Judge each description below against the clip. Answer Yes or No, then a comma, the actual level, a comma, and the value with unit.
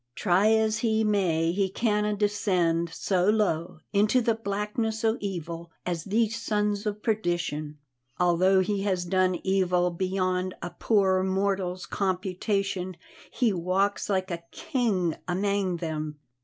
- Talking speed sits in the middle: No, slow, 130 wpm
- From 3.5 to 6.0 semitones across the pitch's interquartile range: No, average, 2.8 semitones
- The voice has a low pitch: No, high, 190 Hz